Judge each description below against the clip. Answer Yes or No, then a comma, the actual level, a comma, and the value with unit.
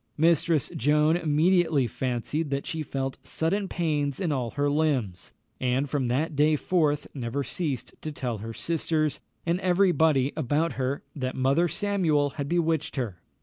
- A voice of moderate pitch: Yes, medium, 150 Hz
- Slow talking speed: No, average, 155 wpm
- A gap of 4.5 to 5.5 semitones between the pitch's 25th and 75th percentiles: No, average, 3.6 semitones